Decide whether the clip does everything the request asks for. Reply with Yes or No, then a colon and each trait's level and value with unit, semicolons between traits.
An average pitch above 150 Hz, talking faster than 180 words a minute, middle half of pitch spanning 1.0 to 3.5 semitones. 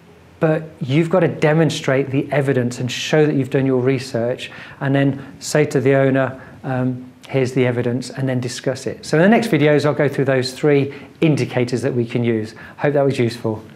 No: low, 135 Hz; fast, 205 wpm; average, 2.8 semitones